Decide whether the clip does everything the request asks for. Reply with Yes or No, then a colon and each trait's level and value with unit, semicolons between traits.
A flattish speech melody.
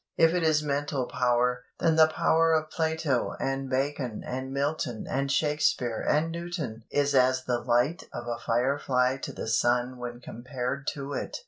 No: average, 3.5 semitones